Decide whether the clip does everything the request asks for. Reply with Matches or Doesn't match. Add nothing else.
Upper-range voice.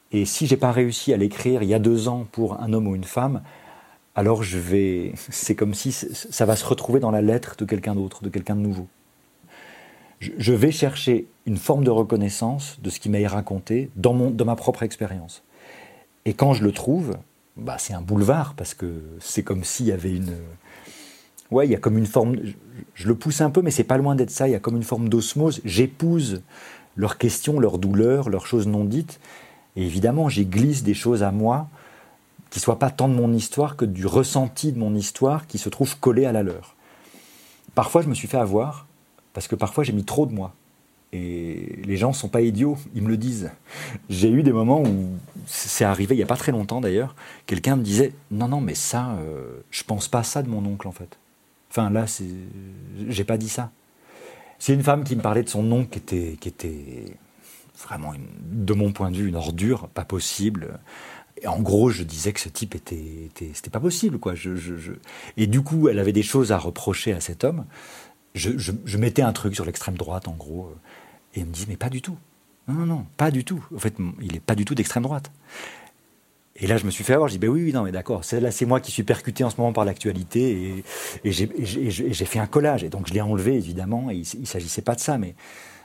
Doesn't match